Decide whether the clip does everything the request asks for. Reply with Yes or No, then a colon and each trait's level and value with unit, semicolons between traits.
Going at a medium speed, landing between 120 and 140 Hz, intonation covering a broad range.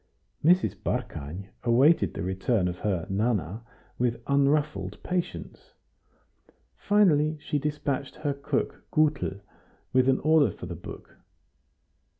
No: slow, 115 wpm; low, 135 Hz; wide, 7.3 semitones